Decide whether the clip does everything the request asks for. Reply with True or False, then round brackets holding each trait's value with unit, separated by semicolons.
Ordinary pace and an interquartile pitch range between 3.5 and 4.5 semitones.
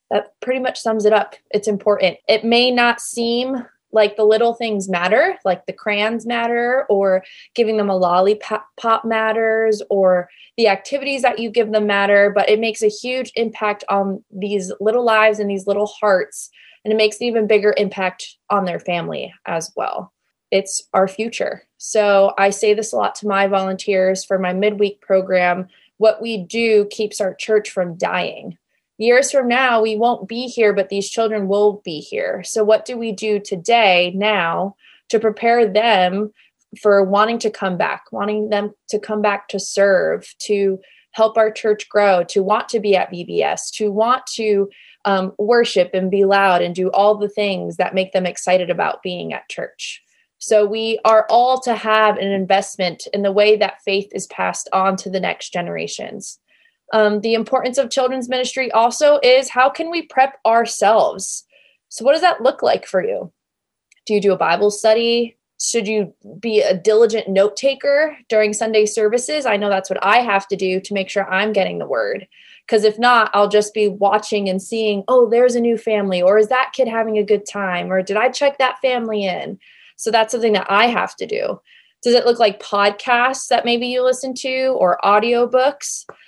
False (190 wpm; 3.0 semitones)